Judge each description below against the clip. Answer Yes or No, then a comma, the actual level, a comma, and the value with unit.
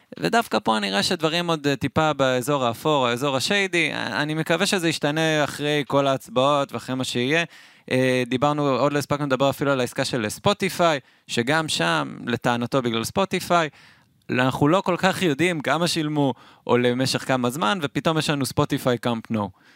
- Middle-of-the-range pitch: Yes, medium, 145 Hz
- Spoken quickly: Yes, fast, 160 wpm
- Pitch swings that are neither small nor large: Yes, average, 4.0 semitones